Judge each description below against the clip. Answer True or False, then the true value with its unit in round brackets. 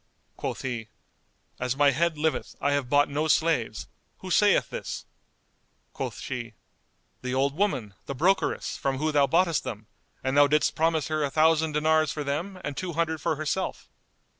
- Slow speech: False (170 wpm)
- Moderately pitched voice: True (150 Hz)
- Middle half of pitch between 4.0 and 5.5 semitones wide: False (2.9 semitones)